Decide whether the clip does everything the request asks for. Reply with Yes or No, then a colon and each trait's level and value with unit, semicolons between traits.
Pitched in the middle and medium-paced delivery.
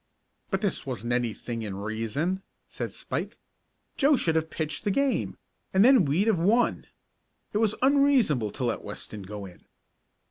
Yes: medium, 160 Hz; average, 155 wpm